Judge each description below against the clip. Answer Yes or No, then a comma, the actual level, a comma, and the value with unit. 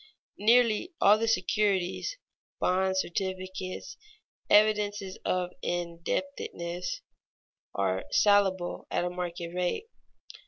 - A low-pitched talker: No, high, 190 Hz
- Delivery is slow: Yes, slow, 85 wpm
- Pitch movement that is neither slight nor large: Yes, average, 3.0 semitones